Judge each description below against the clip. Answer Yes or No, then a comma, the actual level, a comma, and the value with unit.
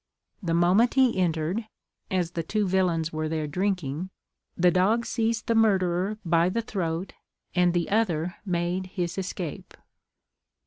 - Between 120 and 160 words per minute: Yes, average, 140 wpm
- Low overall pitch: No, medium, 180 Hz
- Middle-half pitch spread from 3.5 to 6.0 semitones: No, average, 3.1 semitones